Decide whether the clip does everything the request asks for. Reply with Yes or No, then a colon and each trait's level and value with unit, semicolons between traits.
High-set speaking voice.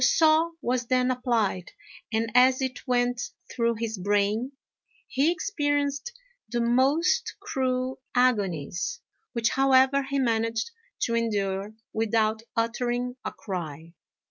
Yes: high, 245 Hz